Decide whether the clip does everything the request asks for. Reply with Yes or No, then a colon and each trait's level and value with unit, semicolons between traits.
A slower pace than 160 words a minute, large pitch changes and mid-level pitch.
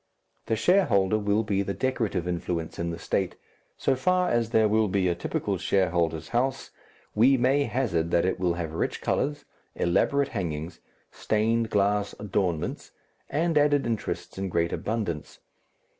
No: average, 150 wpm; wide, 6.2 semitones; low, 105 Hz